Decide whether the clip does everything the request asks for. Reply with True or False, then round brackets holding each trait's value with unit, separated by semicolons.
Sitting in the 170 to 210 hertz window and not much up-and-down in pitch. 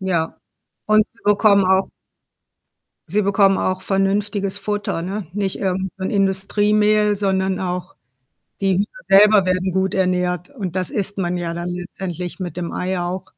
True (190 Hz; 1.9 semitones)